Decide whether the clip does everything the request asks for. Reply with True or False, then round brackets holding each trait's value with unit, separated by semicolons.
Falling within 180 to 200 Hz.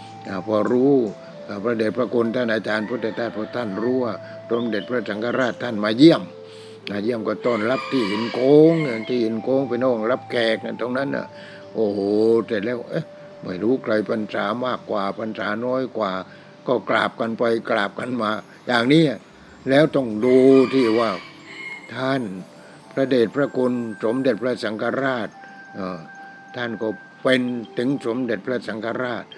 False (115 Hz)